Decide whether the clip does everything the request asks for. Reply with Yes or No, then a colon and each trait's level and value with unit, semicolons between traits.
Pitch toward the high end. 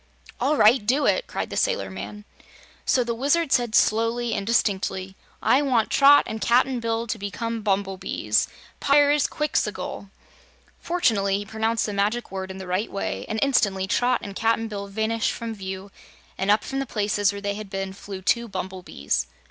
Yes: high, 220 Hz